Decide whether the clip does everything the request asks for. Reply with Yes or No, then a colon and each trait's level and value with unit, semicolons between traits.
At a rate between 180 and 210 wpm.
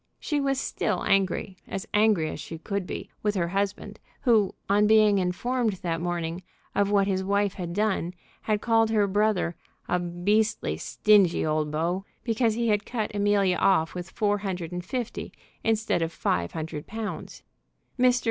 No: average, 165 wpm